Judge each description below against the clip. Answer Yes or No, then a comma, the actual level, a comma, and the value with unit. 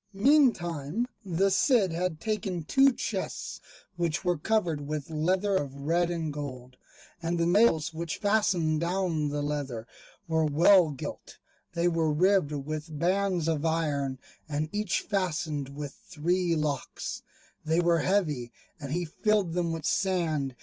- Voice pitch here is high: No, medium, 165 Hz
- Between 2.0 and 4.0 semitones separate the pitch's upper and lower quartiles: Yes, average, 3.7 semitones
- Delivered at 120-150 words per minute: Yes, average, 145 wpm